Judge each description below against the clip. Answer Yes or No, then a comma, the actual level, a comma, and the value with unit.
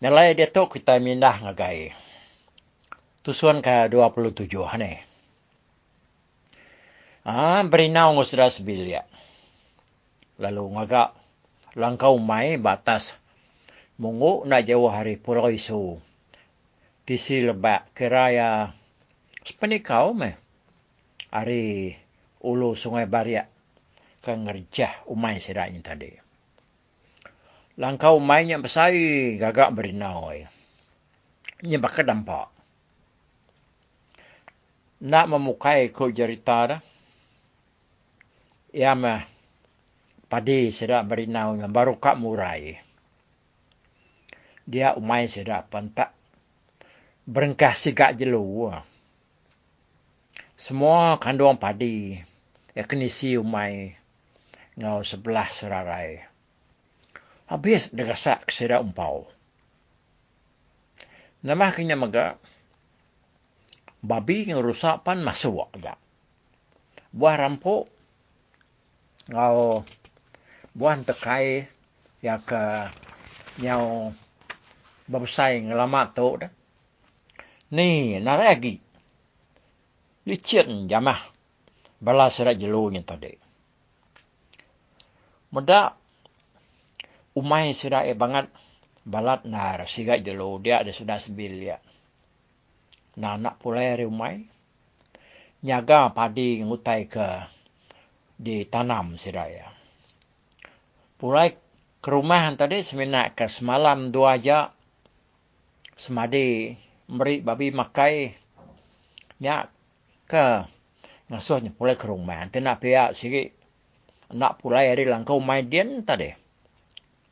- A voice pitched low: Yes, low, 120 Hz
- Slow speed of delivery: Yes, slow, 85 wpm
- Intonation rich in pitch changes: No, average, 4.2 semitones